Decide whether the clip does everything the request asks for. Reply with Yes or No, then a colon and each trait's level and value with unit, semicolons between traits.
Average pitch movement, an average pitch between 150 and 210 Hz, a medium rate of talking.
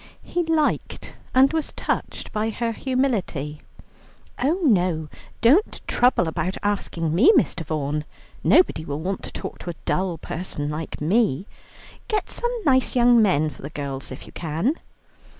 No: wide, 8.7 semitones; high, 190 Hz; average, 150 wpm